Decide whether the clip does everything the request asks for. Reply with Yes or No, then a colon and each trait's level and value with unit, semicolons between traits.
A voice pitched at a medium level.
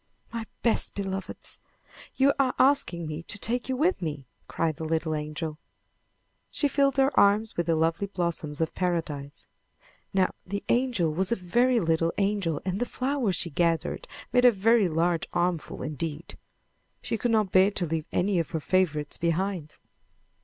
Yes: medium, 180 Hz